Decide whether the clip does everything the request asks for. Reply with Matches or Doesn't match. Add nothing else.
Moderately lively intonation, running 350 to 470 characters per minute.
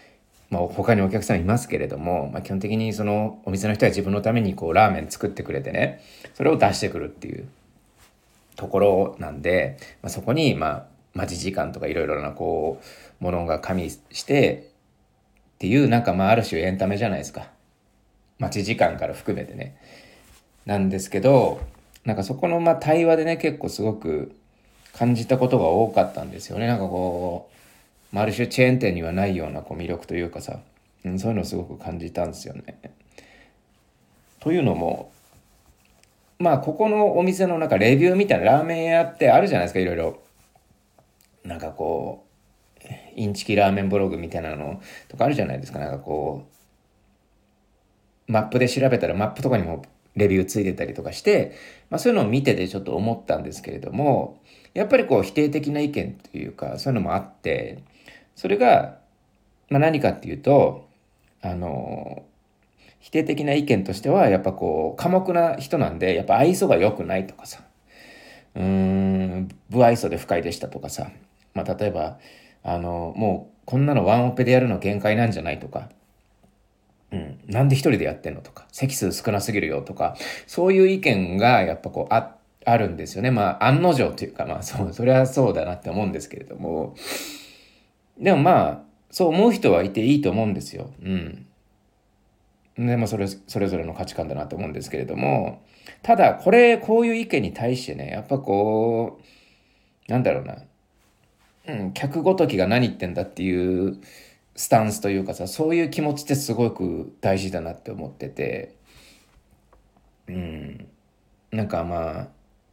Doesn't match